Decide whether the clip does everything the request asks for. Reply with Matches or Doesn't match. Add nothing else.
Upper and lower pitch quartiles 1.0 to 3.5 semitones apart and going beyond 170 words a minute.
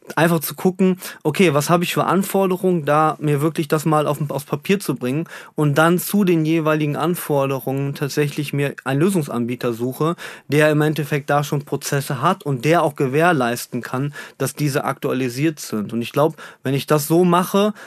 Matches